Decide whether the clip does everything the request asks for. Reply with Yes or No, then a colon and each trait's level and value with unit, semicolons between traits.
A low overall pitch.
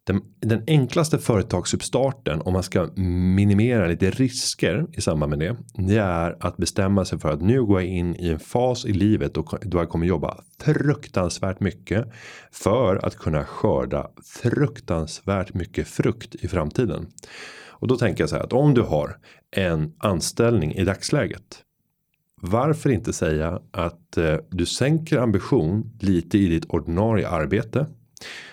Yes: low, 100 Hz